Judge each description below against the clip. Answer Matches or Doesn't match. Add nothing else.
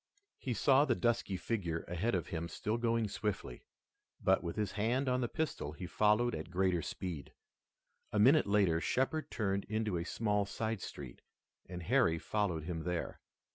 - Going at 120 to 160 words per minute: Doesn't match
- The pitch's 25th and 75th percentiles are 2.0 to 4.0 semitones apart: Doesn't match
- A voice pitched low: Matches